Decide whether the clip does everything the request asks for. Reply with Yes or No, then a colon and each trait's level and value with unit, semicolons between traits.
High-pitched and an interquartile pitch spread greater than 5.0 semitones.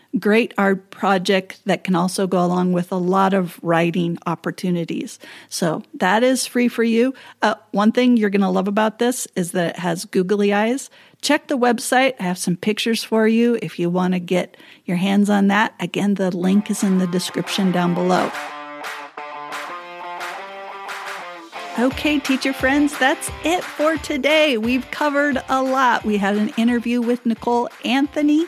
Yes: high, 205 Hz; wide, 5.5 semitones